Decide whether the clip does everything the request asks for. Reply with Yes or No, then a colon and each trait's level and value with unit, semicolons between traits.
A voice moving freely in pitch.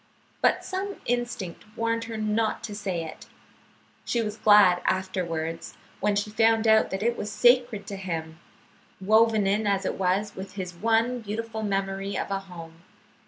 No: average, 3.0 semitones